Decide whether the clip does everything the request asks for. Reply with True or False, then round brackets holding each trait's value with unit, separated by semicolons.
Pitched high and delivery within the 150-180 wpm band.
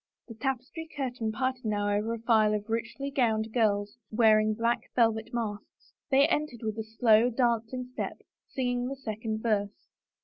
True (230 Hz; 165 wpm)